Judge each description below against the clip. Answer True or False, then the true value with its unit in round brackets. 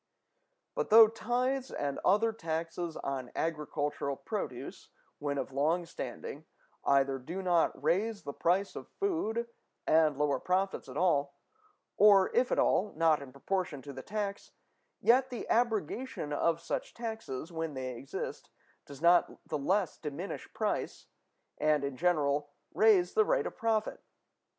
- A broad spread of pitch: True (6.7 semitones)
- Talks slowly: False (145 wpm)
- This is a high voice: False (165 Hz)